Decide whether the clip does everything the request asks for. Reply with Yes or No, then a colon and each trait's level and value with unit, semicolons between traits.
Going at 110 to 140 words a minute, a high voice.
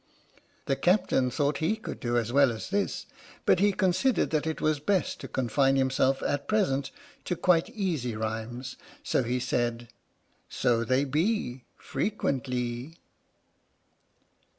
No: slow, 135 wpm; low, 135 Hz